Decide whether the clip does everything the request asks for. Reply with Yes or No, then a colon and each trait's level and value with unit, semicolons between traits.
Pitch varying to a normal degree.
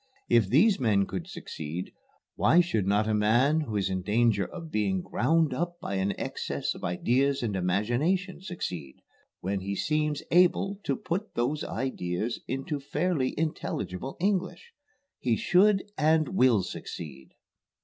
No: wide, 8.5 semitones